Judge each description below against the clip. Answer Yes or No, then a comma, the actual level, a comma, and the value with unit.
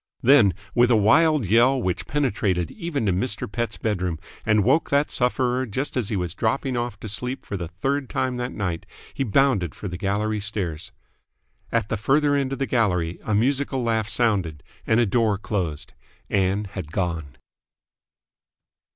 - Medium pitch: No, low, 110 Hz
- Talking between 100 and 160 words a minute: No, average, 170 wpm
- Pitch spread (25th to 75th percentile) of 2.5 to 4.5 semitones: No, average, 5.2 semitones